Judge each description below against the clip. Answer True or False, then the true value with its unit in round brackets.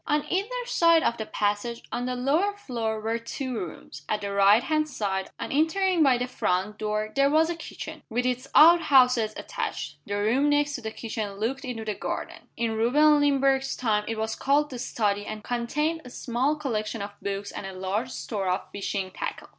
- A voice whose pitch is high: True (240 Hz)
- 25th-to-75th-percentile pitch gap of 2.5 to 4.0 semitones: False (5.5 semitones)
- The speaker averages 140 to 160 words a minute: False (200 wpm)